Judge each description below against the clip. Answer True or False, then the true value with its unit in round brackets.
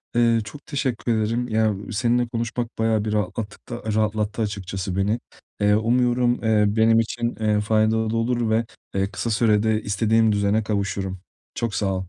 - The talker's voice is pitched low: True (110 Hz)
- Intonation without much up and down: True (2.0 semitones)